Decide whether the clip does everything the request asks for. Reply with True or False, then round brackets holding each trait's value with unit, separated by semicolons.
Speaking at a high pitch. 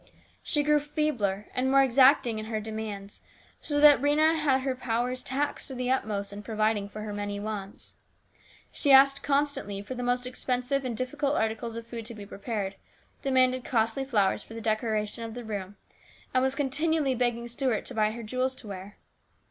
True (240 Hz)